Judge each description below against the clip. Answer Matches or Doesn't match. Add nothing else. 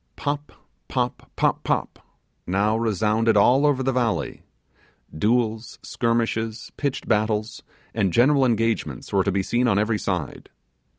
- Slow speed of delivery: Matches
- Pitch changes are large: Doesn't match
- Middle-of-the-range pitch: Doesn't match